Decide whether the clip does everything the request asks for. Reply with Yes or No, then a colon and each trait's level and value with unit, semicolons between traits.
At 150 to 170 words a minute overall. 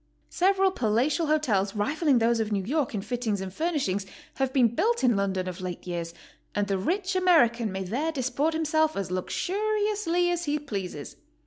No: average, 180 wpm